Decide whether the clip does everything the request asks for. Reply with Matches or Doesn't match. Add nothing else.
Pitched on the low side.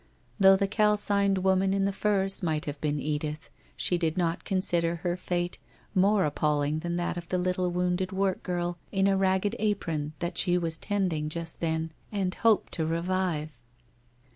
Doesn't match